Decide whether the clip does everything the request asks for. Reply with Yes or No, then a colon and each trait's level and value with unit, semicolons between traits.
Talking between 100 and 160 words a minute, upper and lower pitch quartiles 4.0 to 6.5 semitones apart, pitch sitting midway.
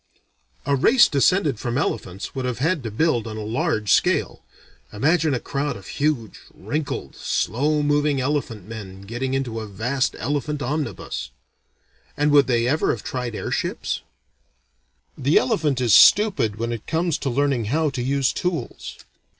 No: average, 155 wpm; average, 4.6 semitones; low, 130 Hz